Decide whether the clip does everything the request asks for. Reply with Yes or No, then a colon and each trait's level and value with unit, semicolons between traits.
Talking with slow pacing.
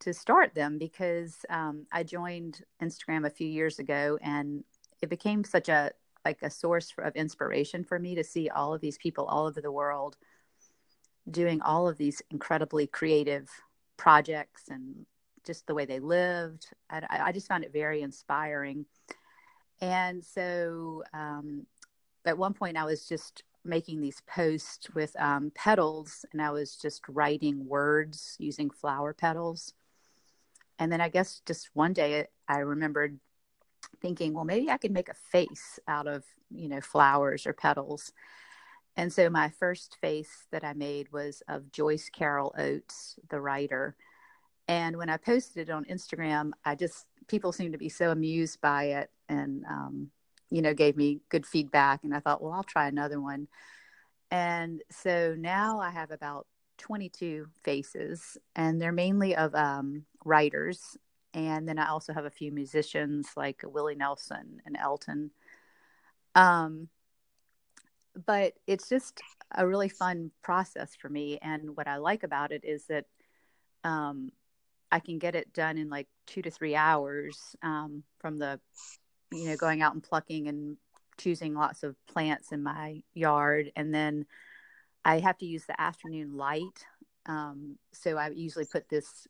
No: average, 160 wpm